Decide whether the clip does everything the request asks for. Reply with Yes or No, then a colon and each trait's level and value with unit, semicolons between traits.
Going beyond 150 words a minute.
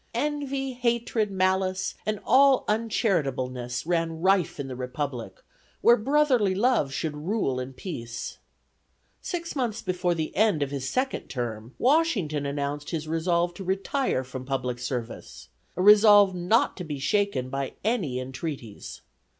No: average, 140 wpm